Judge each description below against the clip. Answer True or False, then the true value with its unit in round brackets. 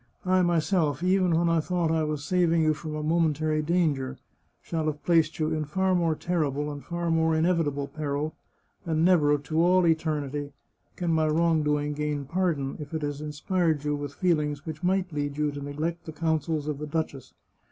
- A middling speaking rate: True (185 wpm)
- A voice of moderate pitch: True (155 Hz)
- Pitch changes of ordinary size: False (2.3 semitones)